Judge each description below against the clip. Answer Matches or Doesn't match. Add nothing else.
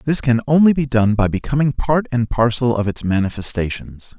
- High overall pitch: Doesn't match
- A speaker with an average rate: Matches